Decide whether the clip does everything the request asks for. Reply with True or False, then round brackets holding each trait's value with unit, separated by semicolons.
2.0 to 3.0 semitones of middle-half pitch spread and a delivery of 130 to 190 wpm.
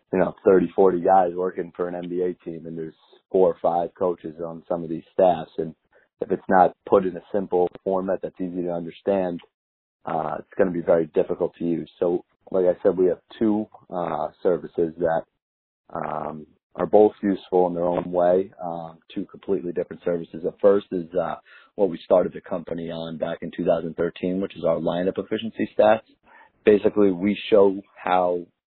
True (2.4 semitones; 185 wpm)